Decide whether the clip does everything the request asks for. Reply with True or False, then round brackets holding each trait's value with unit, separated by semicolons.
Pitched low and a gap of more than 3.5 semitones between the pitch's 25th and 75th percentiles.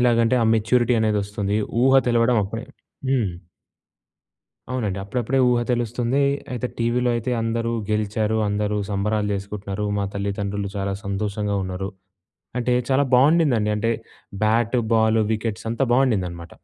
False (110 Hz; 2.9 semitones)